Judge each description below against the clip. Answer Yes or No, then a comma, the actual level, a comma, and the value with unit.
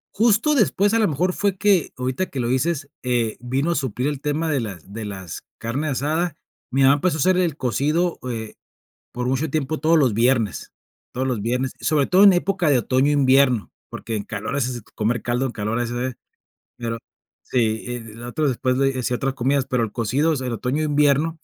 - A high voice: No, low, 135 Hz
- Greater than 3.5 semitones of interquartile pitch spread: Yes, average, 4.4 semitones